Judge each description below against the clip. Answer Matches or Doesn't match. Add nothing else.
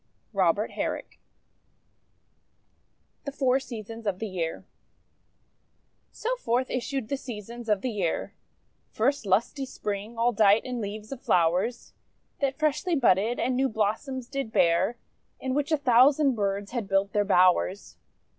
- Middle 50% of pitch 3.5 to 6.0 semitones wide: Matches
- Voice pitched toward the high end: Matches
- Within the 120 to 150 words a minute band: Matches